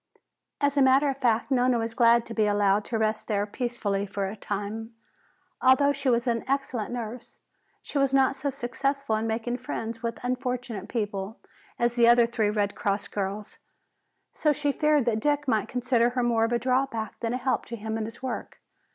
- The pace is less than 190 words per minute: No, average, 195 wpm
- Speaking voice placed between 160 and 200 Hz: No, high, 235 Hz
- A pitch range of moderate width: Yes, average, 3.0 semitones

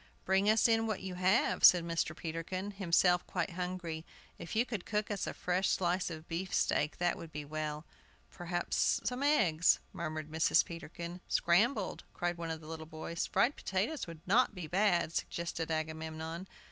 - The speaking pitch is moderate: Yes, medium, 175 Hz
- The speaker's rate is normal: Yes, average, 170 wpm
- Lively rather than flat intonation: No, average, 2.9 semitones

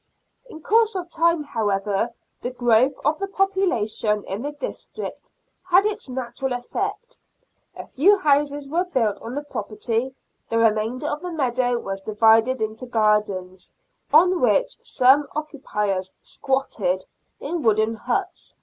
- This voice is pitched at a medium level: No, very high, 255 Hz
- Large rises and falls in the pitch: Yes, wide, 6.2 semitones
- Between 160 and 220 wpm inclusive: No, average, 145 wpm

